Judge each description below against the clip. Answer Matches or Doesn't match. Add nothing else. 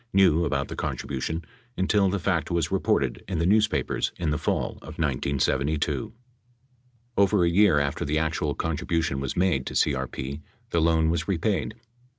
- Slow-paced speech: Doesn't match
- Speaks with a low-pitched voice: Matches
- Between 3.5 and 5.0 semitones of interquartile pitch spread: Matches